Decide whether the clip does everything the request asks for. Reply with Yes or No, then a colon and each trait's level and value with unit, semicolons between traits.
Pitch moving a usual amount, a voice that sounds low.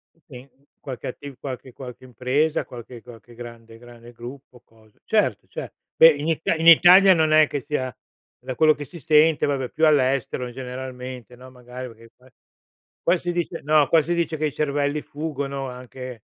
Yes: average, 3.7 semitones; low, 130 Hz